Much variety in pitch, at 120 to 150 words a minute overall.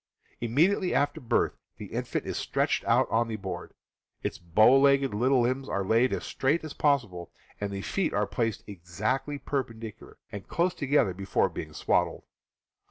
No: wide, 5.8 semitones; average, 160 wpm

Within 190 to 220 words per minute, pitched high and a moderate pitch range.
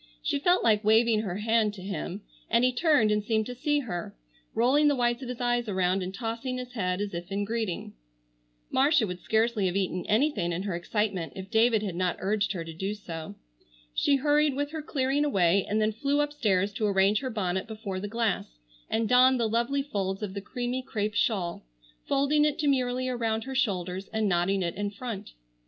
Yes: fast, 205 wpm; high, 220 Hz; average, 4.6 semitones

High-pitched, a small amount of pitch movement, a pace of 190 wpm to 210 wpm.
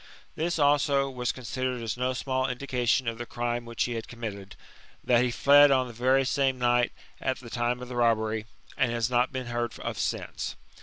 No: low, 125 Hz; narrow, 1.7 semitones; average, 200 wpm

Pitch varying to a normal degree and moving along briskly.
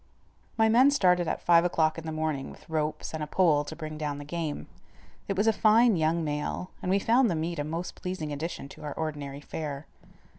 Yes: average, 3.2 semitones; fast, 220 wpm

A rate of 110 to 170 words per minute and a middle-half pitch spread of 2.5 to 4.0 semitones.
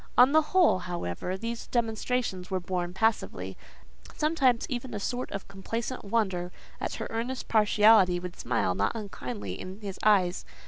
No: average, 150 wpm; average, 4.7 semitones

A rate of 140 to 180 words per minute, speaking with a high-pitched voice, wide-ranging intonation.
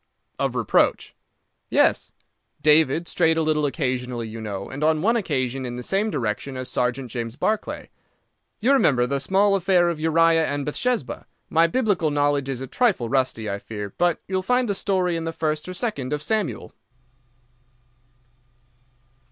No: average, 165 wpm; medium, 155 Hz; wide, 6.1 semitones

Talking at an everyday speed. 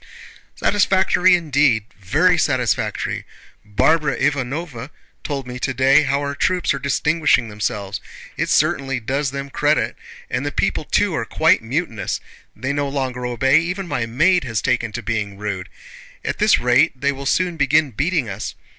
Yes: average, 150 wpm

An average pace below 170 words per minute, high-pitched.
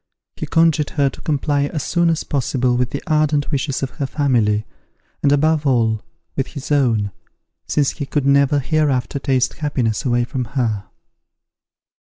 No: average, 155 wpm; medium, 140 Hz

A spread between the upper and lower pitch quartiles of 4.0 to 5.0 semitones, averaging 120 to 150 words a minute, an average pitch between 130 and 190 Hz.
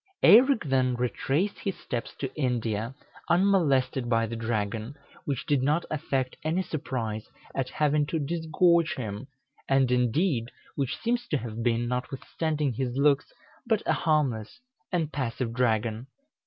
Yes: average, 4.6 semitones; average, 140 wpm; low, 135 Hz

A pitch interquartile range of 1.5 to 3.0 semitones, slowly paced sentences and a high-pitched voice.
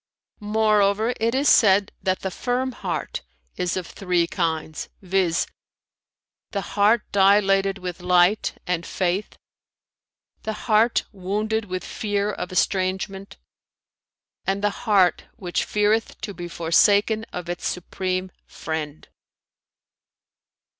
Yes: average, 2.7 semitones; slow, 115 wpm; high, 195 Hz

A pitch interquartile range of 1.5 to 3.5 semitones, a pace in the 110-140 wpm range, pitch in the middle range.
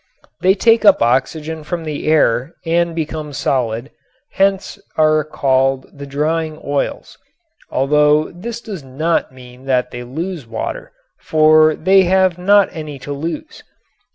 No: average, 4.0 semitones; slow, 135 wpm; medium, 155 Hz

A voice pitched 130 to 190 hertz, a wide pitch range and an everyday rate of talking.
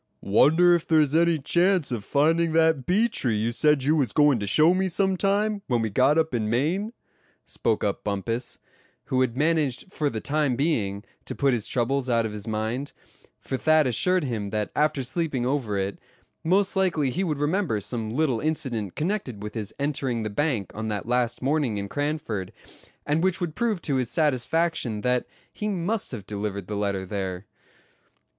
Yes: low, 135 Hz; wide, 6.5 semitones; average, 185 wpm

